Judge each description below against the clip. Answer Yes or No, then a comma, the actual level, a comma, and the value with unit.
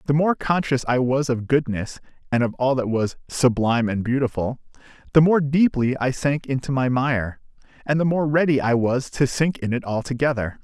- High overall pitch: No, low, 130 Hz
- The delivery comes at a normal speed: Yes, average, 190 wpm